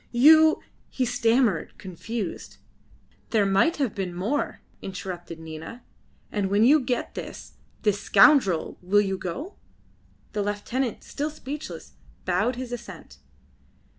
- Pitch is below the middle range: No, high, 215 Hz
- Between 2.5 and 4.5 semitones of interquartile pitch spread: No, average, 5.2 semitones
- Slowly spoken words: Yes, slow, 125 wpm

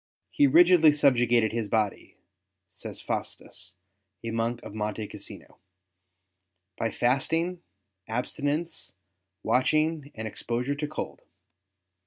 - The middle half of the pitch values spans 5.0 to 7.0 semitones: Yes, wide, 5.4 semitones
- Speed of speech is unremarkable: No, slow, 105 wpm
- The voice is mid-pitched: No, low, 120 Hz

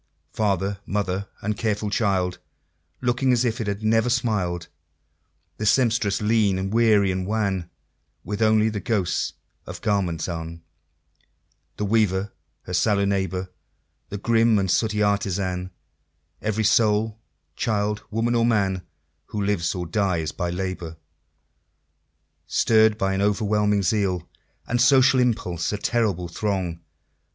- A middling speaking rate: No, slow, 130 wpm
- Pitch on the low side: Yes, low, 105 Hz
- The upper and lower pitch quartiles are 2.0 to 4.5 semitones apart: Yes, average, 2.8 semitones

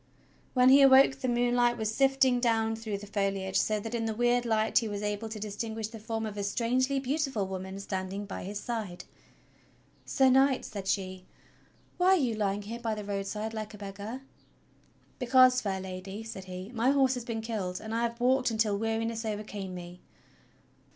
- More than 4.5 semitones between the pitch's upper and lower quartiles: No, average, 3.3 semitones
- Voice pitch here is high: Yes, high, 220 Hz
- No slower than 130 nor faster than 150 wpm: No, average, 190 wpm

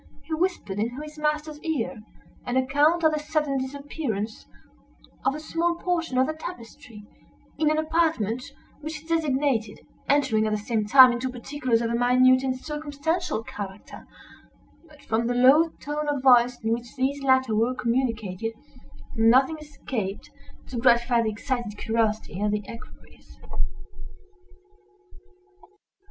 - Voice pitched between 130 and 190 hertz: No, very high, 260 Hz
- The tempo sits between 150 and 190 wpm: No, average, 140 wpm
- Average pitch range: Yes, average, 4.8 semitones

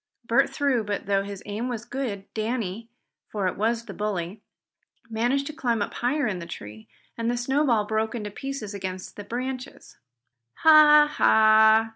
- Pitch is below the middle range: No, high, 220 Hz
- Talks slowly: No, average, 165 wpm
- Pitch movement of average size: Yes, average, 3.7 semitones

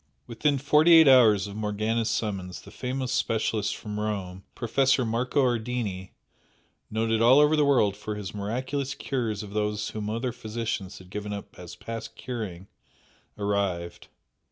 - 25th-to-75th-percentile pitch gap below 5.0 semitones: Yes, average, 3.5 semitones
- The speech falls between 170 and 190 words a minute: No, average, 150 wpm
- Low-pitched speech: Yes, low, 110 Hz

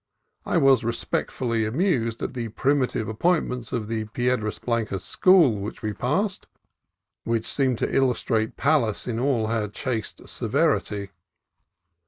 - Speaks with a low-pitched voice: Yes, low, 115 Hz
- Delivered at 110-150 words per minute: Yes, average, 140 wpm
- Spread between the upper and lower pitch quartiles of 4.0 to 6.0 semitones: No, average, 3.3 semitones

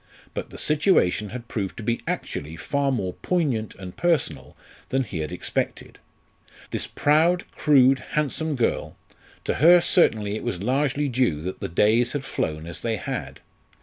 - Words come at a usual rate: Yes, average, 160 wpm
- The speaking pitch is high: No, low, 120 Hz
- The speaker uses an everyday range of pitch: No, wide, 7.2 semitones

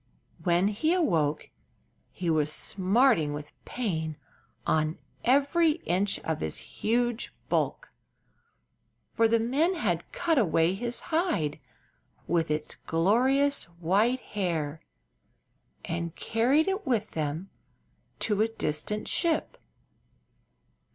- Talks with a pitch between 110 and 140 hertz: No, high, 200 Hz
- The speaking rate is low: Yes, slow, 105 wpm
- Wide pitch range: Yes, wide, 7.6 semitones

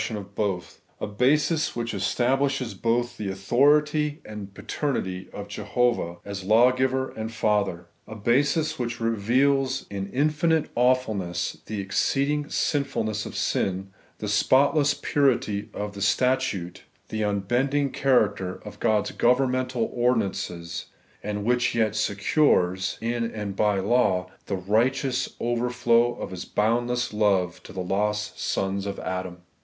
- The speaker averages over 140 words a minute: No, slow, 135 wpm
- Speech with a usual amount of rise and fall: Yes, average, 4.4 semitones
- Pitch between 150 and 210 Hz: No, low, 110 Hz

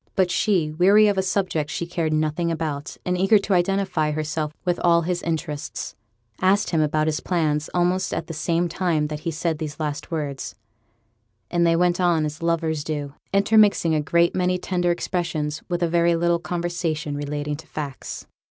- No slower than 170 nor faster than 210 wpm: Yes, average, 180 wpm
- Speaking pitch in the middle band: Yes, medium, 170 Hz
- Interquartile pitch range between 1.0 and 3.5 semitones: Yes, narrow, 2.5 semitones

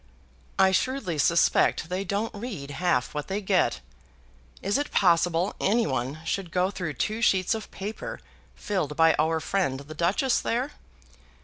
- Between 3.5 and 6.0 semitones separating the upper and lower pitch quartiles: Yes, average, 4.4 semitones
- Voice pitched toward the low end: No, medium, 185 Hz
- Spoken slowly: No, average, 150 wpm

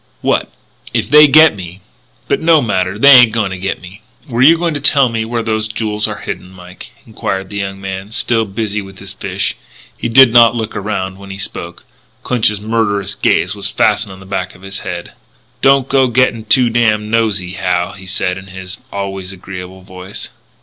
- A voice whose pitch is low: Yes, low, 105 Hz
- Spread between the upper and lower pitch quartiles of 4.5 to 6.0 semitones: No, average, 3.4 semitones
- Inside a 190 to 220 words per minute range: Yes, fast, 205 wpm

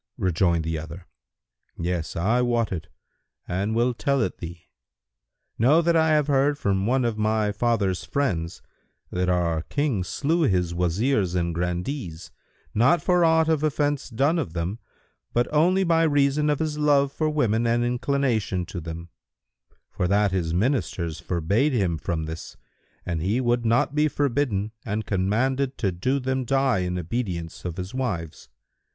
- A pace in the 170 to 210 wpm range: No, average, 160 wpm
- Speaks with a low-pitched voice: Yes, low, 110 Hz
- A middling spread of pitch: No, wide, 7.8 semitones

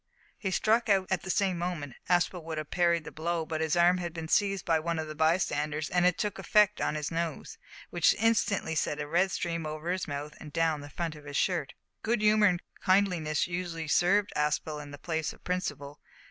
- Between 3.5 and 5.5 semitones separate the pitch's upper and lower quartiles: No, average, 3.0 semitones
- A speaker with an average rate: No, fast, 215 wpm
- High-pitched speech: No, medium, 170 Hz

